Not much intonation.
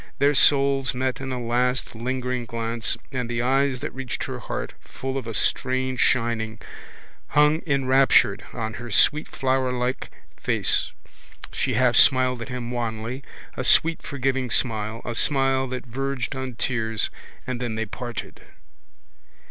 Yes: narrow, 2.1 semitones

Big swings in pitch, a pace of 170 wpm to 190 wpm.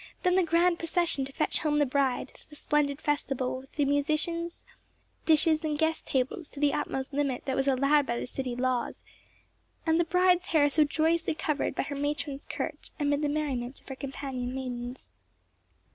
No: average, 2.9 semitones; average, 180 wpm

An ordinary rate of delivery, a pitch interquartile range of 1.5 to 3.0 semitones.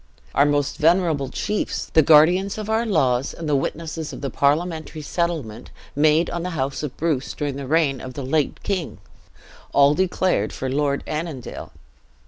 No: average, 165 wpm; average, 3.4 semitones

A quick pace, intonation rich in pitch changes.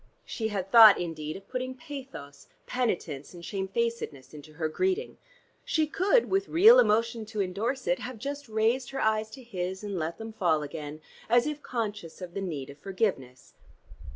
No: average, 175 wpm; wide, 7.1 semitones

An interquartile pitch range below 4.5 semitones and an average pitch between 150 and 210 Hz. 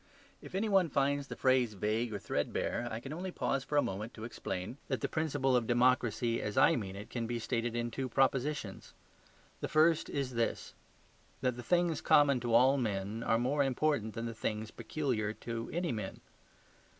No: average, 3.9 semitones; low, 120 Hz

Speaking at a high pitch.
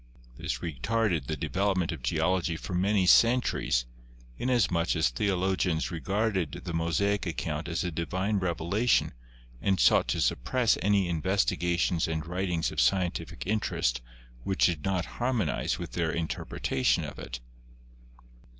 No: very low, 90 Hz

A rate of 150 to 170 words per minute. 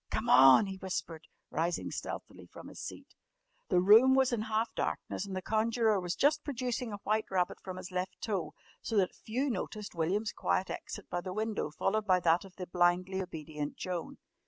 No: average, 190 wpm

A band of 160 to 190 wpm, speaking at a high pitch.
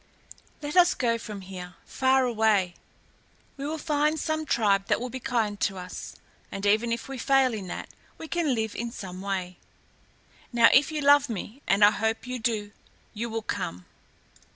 Yes: average, 180 wpm; high, 230 Hz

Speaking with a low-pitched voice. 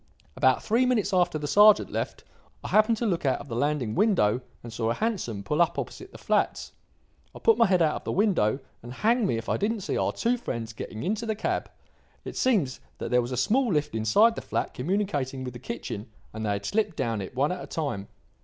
No: medium, 150 Hz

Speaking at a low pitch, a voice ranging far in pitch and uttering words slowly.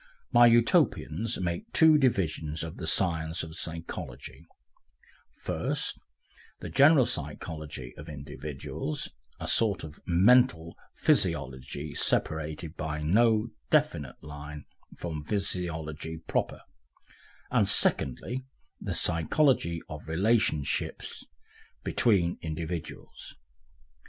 Yes: very low, 80 Hz; wide, 5.7 semitones; slow, 90 wpm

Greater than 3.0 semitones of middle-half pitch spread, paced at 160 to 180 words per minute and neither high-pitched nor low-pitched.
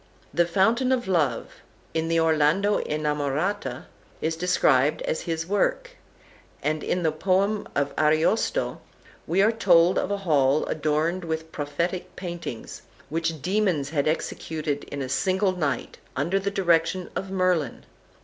No: average, 3.8 semitones; average, 140 wpm; medium, 165 Hz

